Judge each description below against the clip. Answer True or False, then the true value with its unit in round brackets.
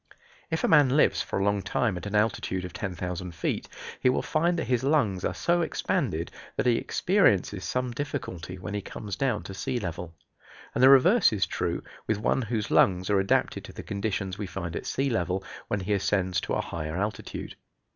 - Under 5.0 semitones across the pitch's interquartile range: False (5.6 semitones)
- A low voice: True (105 Hz)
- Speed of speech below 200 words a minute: False (205 wpm)